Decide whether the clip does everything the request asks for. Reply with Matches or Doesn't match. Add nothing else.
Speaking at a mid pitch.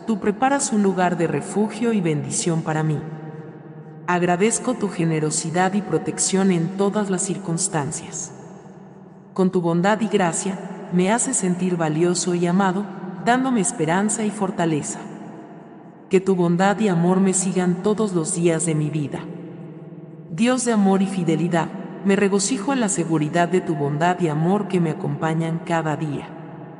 Matches